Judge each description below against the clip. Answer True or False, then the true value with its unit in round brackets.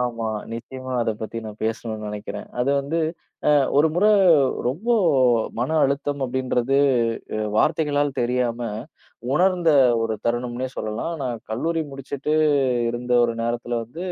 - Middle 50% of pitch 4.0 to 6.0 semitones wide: False (3.6 semitones)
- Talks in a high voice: False (125 Hz)